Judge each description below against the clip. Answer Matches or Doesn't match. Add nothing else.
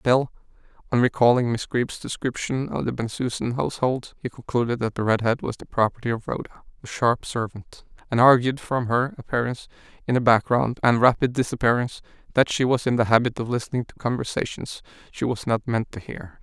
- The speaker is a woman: Doesn't match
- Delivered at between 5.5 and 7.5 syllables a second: Matches